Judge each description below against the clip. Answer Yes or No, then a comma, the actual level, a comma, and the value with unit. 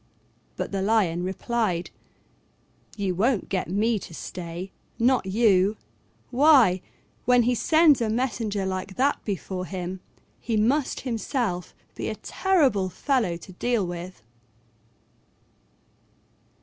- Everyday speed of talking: No, slow, 115 wpm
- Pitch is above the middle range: Yes, high, 205 Hz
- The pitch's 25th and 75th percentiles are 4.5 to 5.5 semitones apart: Yes, average, 4.9 semitones